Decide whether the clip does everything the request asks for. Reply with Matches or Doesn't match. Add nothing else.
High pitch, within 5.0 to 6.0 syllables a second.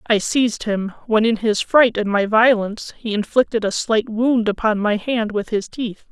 Doesn't match